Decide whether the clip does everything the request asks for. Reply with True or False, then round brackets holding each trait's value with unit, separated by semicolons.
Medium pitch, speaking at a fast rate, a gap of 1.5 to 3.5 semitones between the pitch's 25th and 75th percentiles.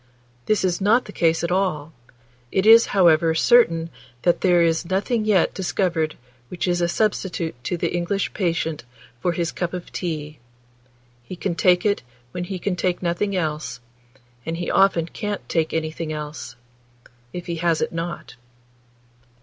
False (175 Hz; 160 wpm; 2.6 semitones)